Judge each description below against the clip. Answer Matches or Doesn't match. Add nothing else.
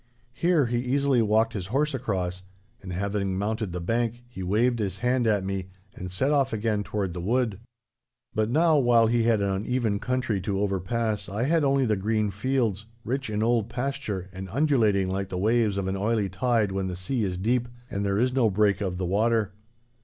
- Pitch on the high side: Doesn't match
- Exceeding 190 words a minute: Matches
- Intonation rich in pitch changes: Doesn't match